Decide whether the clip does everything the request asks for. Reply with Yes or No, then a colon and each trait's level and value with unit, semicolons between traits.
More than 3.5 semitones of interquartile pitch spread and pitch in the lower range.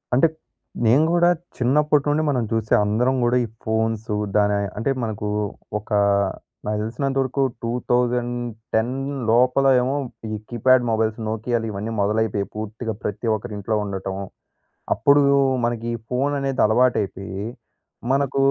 No: average, 3.1 semitones; low, 115 Hz